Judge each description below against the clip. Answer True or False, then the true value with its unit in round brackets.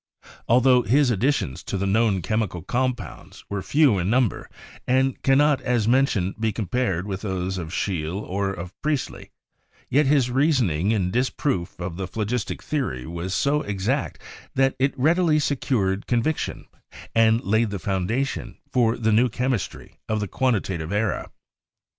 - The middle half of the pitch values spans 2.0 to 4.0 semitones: False (5.4 semitones)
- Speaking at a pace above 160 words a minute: False (150 wpm)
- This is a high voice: False (110 Hz)